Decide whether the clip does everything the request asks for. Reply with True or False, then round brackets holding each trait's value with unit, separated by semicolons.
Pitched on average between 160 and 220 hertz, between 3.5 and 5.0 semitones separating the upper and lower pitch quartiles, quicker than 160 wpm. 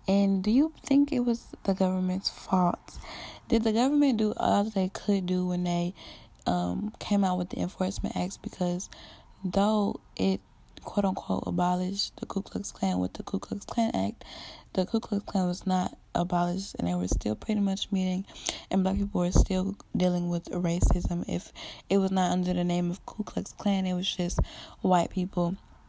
False (185 Hz; 2.4 semitones; 185 wpm)